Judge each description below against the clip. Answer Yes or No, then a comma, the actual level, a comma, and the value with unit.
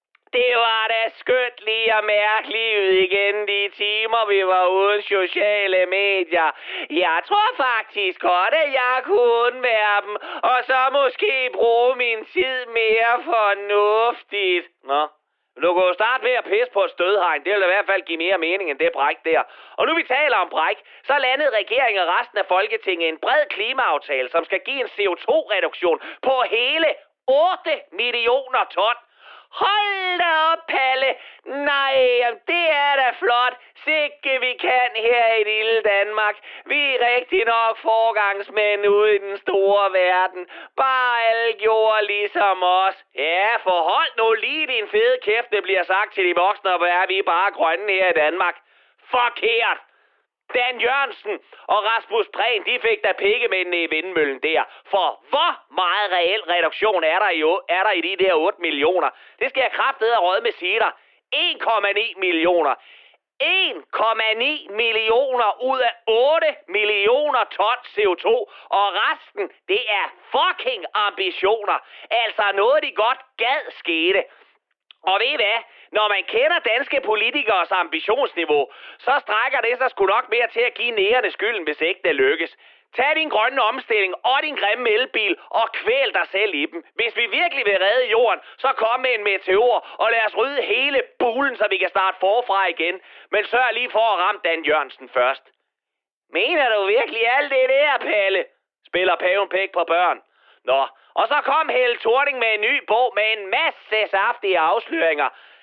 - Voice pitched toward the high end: Yes, high, 245 Hz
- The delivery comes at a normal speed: Yes, average, 165 wpm